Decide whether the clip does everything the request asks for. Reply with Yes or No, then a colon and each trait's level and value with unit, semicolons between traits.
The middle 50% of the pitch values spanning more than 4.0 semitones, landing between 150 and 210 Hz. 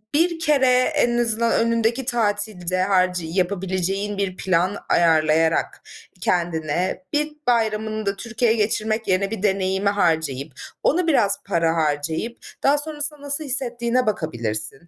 Yes: average, 5.2 semitones; high, 205 Hz